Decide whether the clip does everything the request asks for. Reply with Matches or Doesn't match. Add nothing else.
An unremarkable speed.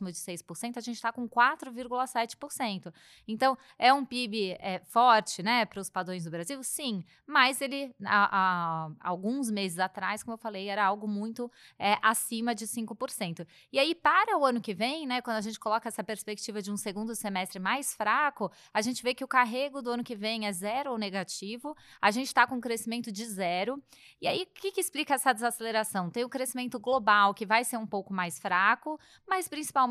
Doesn't match